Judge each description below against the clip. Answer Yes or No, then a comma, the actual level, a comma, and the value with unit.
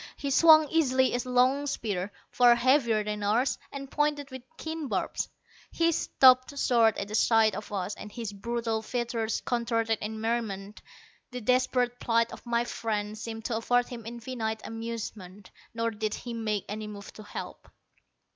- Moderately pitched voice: No, high, 230 Hz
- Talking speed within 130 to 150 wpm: No, average, 165 wpm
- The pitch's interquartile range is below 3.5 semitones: Yes, average, 2.8 semitones